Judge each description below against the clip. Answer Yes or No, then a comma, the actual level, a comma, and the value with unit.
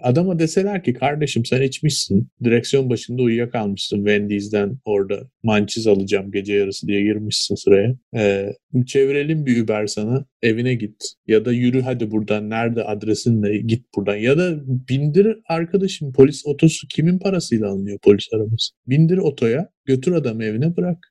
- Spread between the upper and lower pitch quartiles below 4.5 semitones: No, wide, 5.5 semitones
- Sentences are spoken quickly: Yes, fast, 145 wpm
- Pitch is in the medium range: No, low, 120 Hz